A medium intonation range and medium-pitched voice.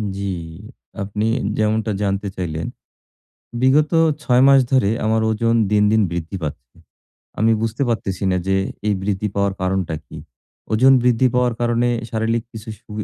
No: average, 3.2 semitones; low, 110 Hz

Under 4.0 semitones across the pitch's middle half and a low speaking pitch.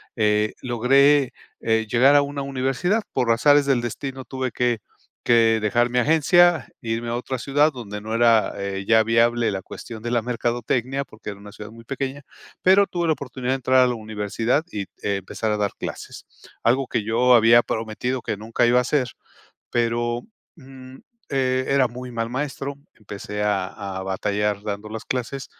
Yes: average, 3.3 semitones; low, 120 Hz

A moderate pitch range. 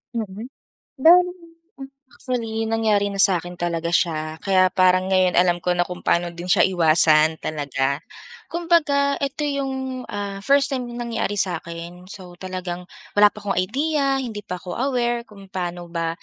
No: wide, 6.1 semitones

